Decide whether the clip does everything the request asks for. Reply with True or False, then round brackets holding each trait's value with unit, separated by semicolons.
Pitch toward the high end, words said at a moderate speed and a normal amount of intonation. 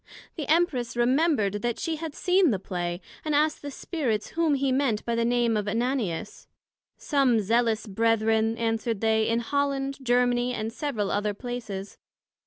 True (240 Hz; 160 wpm; 4.1 semitones)